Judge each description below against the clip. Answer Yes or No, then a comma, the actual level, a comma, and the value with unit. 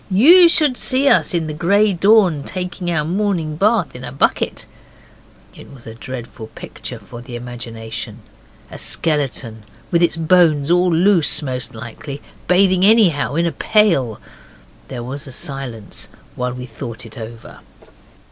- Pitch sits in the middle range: Yes, medium, 150 Hz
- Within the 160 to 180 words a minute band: No, average, 150 wpm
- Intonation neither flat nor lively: No, wide, 7.0 semitones